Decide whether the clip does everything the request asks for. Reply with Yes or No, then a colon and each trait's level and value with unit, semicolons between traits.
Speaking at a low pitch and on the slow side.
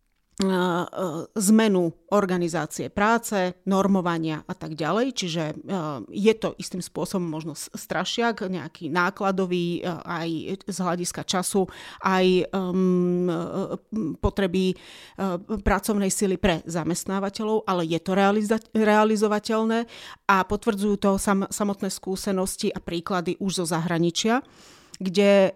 No: high, 190 Hz; slow, 95 wpm